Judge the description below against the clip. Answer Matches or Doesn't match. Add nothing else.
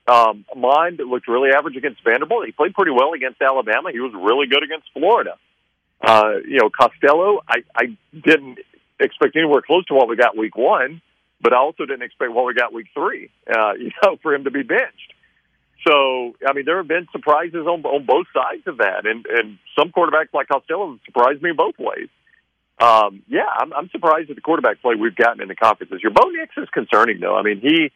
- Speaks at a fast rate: Matches